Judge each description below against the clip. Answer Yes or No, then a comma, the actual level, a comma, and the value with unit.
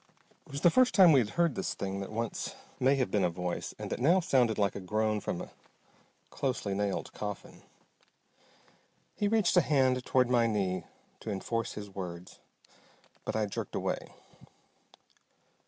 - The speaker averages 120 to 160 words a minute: No, average, 170 wpm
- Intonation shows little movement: No, wide, 5.4 semitones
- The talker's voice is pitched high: No, low, 115 Hz